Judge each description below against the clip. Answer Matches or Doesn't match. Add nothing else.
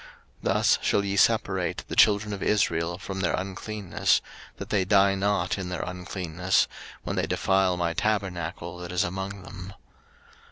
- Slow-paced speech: Doesn't match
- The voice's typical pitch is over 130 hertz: Doesn't match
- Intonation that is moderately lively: Doesn't match